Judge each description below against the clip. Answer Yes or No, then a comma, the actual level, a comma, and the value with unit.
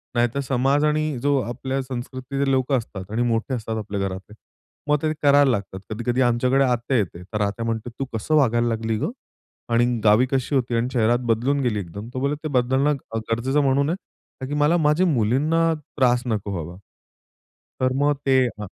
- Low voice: Yes, low, 125 Hz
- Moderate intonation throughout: Yes, average, 3.6 semitones